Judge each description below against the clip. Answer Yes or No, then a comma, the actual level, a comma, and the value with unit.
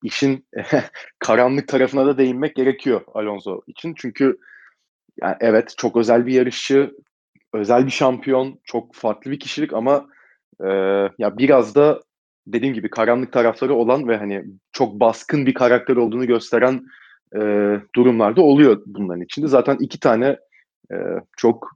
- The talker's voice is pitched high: No, low, 125 Hz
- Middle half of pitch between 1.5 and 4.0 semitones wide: Yes, average, 2.8 semitones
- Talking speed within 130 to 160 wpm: Yes, fast, 140 wpm